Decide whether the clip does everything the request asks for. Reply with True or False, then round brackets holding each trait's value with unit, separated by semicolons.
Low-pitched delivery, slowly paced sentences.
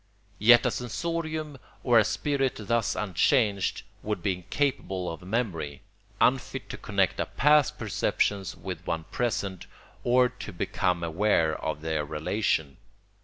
True (105 Hz; 130 wpm)